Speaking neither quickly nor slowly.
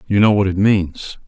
No: fast, 235 wpm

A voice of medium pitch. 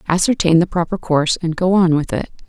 Yes: medium, 170 Hz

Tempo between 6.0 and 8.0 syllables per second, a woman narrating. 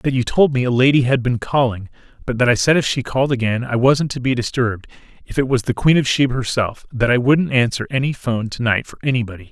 No: 6.3 syllables/s; male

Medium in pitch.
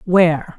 Yes: medium, 170 Hz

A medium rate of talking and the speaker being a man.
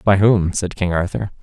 No: fast, 210 wpm; male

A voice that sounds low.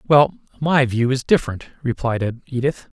Yes: low, 130 Hz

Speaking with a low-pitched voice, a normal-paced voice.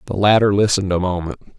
Yes: very low, 95 Hz; average, 190 wpm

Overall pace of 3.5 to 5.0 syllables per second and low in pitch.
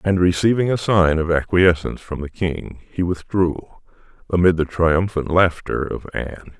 Yes: 4.9 syllables/s; very low, 85 Hz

